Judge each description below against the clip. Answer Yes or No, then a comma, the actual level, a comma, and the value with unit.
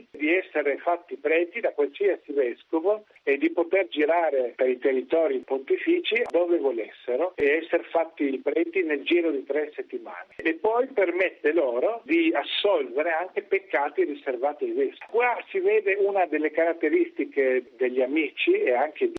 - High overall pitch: Yes, high, 245 Hz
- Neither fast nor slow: Yes, average, 150 wpm